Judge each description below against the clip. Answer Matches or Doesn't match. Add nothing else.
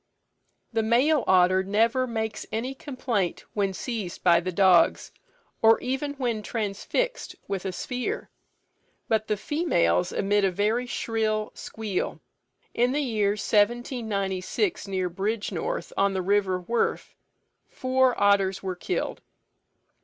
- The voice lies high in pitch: Matches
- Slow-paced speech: Matches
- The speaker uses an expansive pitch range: Doesn't match